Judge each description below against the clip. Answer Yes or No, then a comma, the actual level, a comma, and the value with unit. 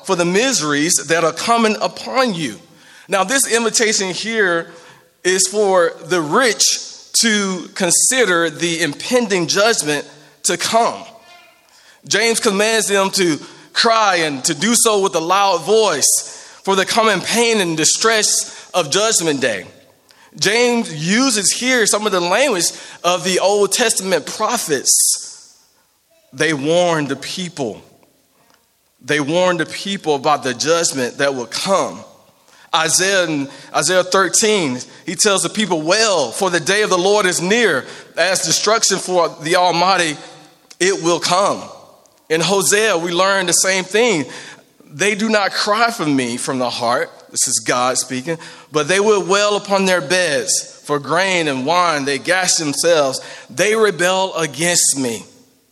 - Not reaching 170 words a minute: Yes, average, 145 wpm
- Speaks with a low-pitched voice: No, medium, 185 Hz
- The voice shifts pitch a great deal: No, average, 4.8 semitones